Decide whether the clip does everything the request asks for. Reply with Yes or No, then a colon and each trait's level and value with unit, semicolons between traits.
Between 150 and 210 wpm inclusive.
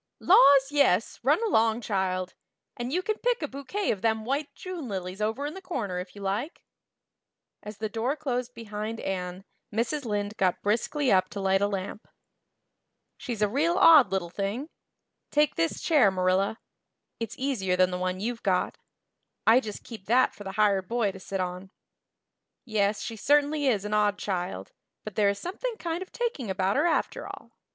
Yes: average, 180 wpm